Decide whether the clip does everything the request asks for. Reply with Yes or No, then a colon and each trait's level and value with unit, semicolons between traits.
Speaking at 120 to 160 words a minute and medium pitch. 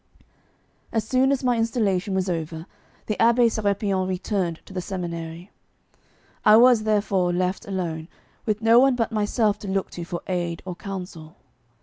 No: average, 155 wpm; high, 195 Hz